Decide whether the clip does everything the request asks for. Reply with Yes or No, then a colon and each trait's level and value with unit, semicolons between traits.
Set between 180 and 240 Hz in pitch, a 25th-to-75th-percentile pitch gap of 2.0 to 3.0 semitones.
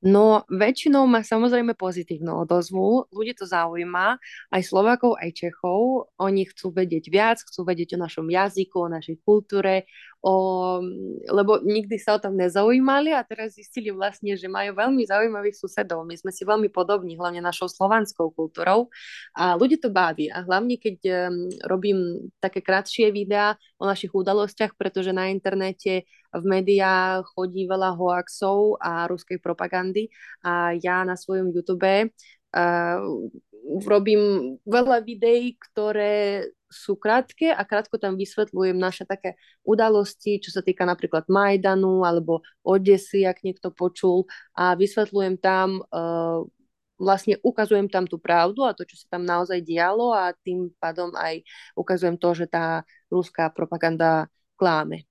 Yes: high, 190 Hz; average, 2.7 semitones